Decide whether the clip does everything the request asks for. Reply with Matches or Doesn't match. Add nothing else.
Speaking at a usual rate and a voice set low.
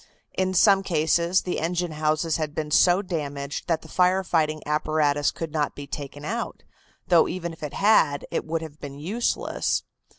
Doesn't match